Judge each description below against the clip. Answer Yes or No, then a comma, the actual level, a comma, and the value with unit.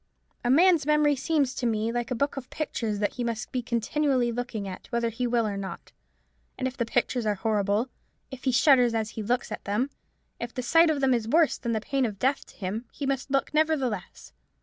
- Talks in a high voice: Yes, high, 245 Hz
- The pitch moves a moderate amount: Yes, average, 3.5 semitones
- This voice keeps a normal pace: No, fast, 225 wpm